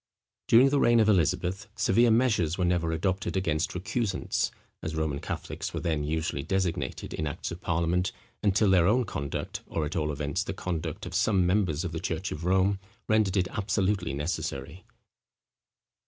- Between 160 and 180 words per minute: Yes, average, 170 wpm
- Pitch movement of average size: Yes, average, 3.9 semitones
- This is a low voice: Yes, very low, 90 Hz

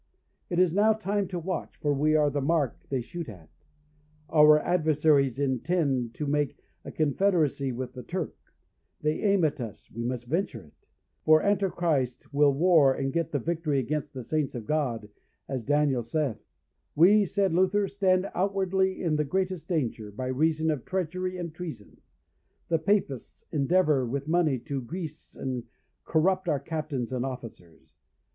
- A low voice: No, medium, 155 Hz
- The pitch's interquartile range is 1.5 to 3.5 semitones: No, average, 5.0 semitones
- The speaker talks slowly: No, average, 160 wpm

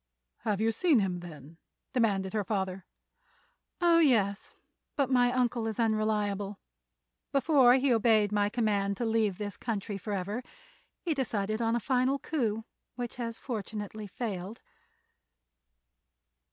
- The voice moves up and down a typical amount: Yes, average, 3.3 semitones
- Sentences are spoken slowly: Yes, slow, 125 wpm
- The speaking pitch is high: Yes, high, 220 Hz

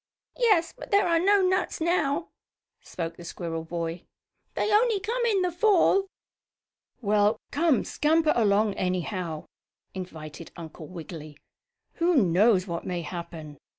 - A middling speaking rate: No, slow, 130 wpm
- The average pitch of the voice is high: Yes, high, 210 Hz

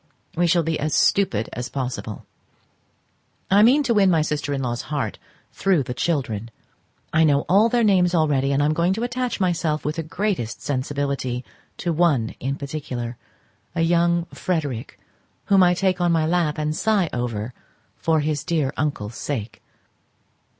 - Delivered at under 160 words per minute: No, average, 165 wpm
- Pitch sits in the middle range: Yes, medium, 155 Hz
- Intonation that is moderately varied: Yes, average, 4.7 semitones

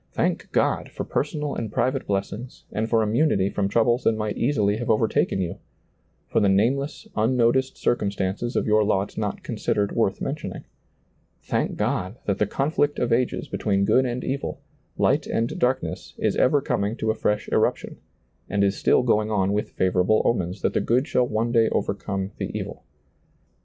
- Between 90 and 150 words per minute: No, average, 175 wpm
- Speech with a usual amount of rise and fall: Yes, average, 3.8 semitones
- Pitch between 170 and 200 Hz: No, low, 110 Hz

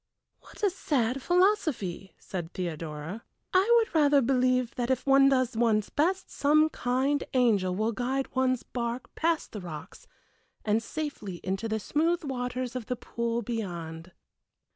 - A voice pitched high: Yes, very high, 250 Hz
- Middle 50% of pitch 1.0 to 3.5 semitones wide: No, average, 5.1 semitones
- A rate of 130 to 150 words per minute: Yes, average, 145 wpm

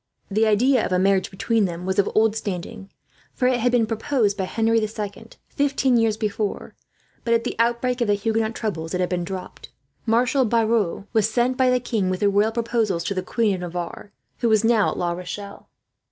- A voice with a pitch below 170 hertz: No, high, 220 Hz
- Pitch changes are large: No, average, 3.2 semitones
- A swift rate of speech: Yes, fast, 210 wpm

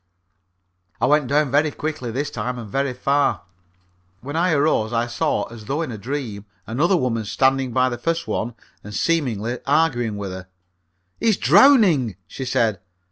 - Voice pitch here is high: No, low, 130 Hz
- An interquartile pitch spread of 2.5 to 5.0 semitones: Yes, average, 4.6 semitones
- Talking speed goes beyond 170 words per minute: No, average, 165 wpm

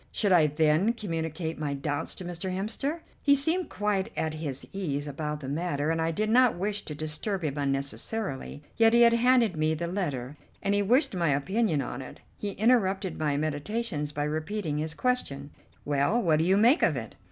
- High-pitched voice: No, medium, 165 Hz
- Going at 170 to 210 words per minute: Yes, average, 195 wpm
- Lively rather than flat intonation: Yes, wide, 6.1 semitones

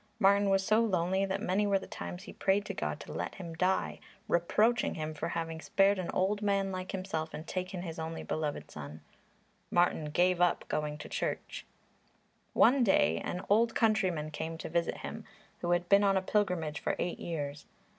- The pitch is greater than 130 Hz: Yes, medium, 185 Hz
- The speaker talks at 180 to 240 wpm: Yes, average, 190 wpm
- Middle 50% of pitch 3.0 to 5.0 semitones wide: Yes, average, 3.4 semitones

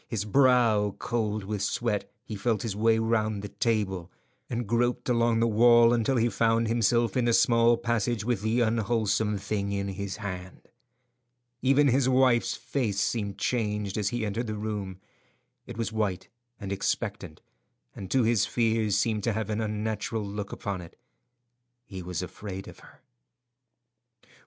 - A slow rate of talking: No, average, 160 wpm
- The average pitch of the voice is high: No, low, 110 Hz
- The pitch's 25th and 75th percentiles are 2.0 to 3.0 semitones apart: Yes, narrow, 2.6 semitones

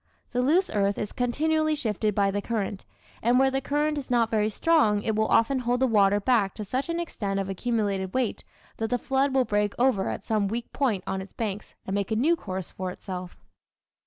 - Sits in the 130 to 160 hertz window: No, high, 225 Hz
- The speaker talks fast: Yes, fast, 220 wpm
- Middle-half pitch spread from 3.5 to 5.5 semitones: Yes, average, 4.7 semitones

